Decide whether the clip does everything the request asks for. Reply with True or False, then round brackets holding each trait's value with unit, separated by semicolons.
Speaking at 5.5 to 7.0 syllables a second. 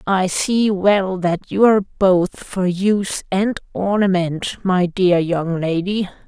False (3.5 syllables/s)